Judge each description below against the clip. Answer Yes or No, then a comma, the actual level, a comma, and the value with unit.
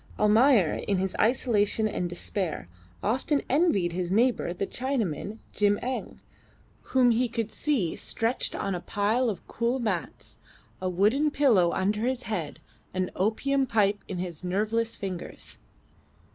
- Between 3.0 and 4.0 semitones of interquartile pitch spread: No, average, 4.8 semitones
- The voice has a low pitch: No, high, 210 Hz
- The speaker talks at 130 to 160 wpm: Yes, average, 145 wpm